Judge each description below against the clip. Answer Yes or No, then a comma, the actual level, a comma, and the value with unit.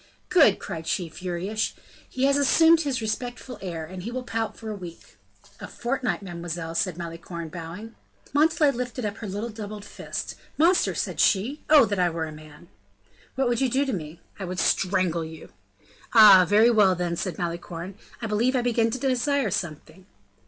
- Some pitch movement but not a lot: No, wide, 6.2 semitones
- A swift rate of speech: No, average, 180 wpm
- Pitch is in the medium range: No, high, 205 Hz